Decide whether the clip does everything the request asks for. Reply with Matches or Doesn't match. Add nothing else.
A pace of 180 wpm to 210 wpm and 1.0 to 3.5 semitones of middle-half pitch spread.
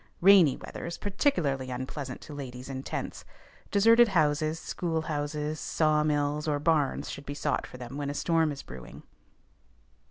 Doesn't match